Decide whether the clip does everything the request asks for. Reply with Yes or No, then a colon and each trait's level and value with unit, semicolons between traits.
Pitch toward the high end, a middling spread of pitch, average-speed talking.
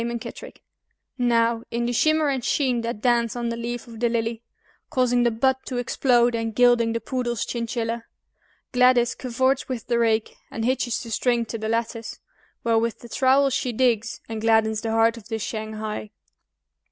No: high, 235 Hz; narrow, 1.4 semitones; average, 175 wpm